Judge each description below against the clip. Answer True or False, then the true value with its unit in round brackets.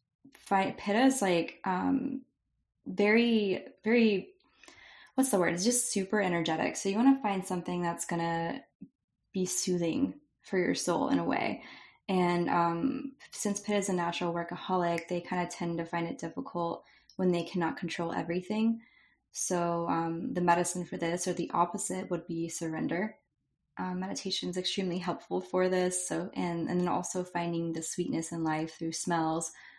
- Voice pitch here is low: False (180 Hz)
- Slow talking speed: False (165 wpm)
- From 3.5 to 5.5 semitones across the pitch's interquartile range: False (2.9 semitones)